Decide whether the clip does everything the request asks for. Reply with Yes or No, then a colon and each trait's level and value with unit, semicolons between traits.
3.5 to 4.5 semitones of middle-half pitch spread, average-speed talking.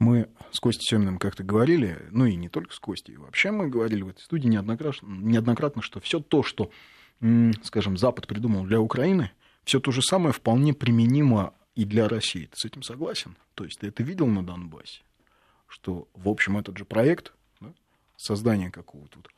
No: average, 3.8 semitones; fast, 185 wpm